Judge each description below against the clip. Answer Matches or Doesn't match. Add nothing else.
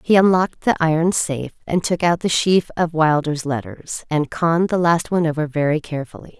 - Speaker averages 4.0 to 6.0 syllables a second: Matches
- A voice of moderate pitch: Matches